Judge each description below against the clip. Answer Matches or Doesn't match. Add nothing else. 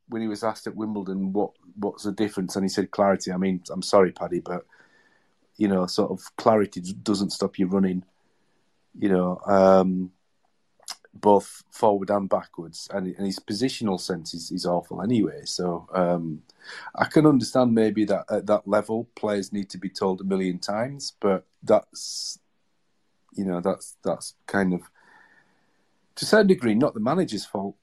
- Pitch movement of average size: Doesn't match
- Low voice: Matches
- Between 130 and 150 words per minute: Doesn't match